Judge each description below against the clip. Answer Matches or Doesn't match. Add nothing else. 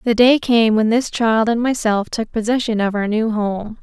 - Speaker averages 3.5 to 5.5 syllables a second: Matches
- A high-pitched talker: Matches